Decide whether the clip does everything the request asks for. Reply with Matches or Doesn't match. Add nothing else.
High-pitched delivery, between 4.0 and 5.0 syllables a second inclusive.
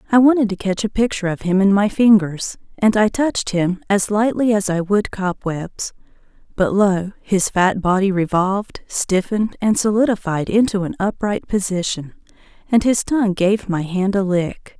Matches